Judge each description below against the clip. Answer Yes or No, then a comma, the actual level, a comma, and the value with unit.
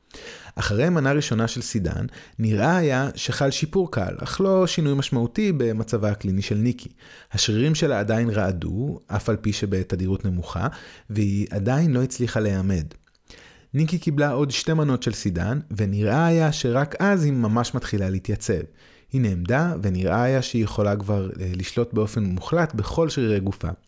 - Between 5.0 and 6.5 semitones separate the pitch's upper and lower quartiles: Yes, wide, 5.5 semitones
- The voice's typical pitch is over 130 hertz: No, low, 115 Hz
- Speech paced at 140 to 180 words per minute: Yes, fast, 150 wpm